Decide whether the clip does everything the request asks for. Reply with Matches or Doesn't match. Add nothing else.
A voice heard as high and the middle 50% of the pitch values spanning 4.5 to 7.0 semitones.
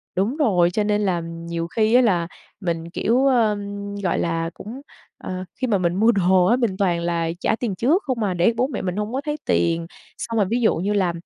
Matches